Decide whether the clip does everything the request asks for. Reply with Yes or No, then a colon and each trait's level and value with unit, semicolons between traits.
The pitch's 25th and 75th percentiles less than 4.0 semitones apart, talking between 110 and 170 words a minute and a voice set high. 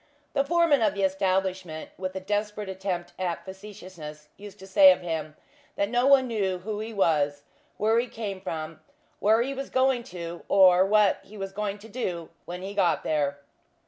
No: average, 3.3 semitones; average, 185 wpm; high, 195 Hz